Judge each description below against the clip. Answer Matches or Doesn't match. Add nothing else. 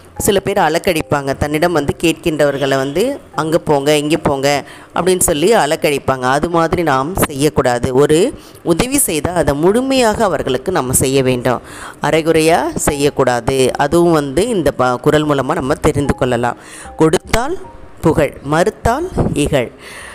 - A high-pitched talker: Doesn't match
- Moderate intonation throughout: Matches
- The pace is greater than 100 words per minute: Matches